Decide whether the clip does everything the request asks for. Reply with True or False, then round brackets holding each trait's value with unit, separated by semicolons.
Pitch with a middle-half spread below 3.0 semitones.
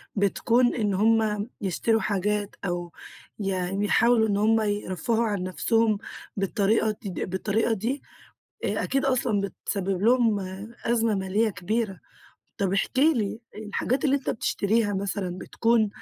True (2.6 semitones)